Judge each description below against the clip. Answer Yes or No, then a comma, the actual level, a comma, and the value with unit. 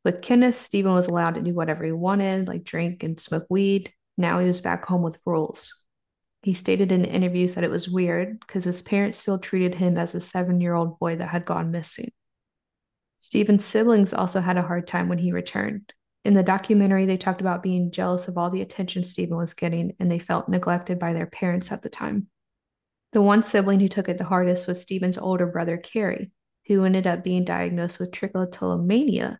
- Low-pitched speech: No, medium, 180 Hz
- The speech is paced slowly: No, average, 200 wpm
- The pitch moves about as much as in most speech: No, narrow, 2.2 semitones